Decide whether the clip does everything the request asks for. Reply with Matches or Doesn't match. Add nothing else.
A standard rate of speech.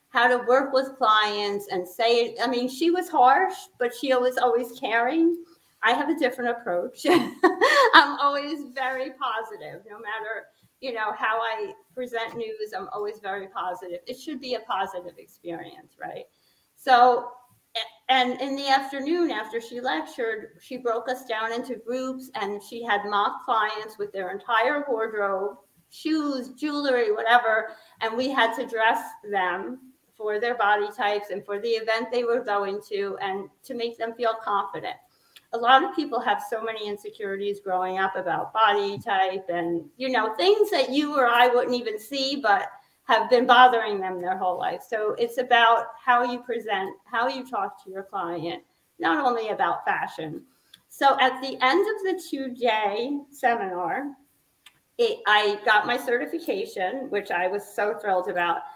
Matches